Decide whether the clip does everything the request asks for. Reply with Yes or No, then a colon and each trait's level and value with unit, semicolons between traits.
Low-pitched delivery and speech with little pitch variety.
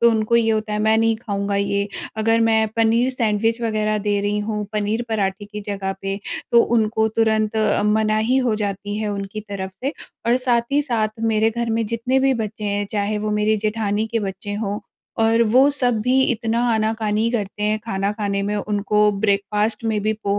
No: high, 215 Hz; narrow, 1.7 semitones